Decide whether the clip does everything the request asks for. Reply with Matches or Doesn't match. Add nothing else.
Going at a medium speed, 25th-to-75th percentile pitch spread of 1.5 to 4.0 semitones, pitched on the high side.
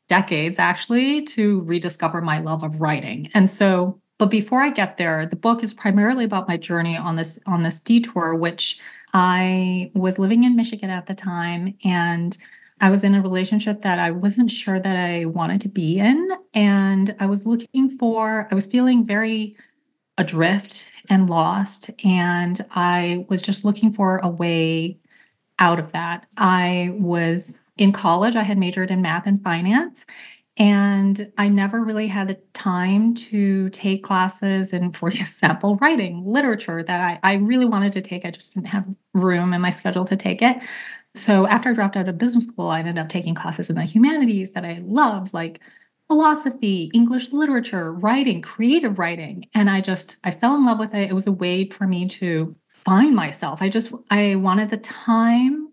Matches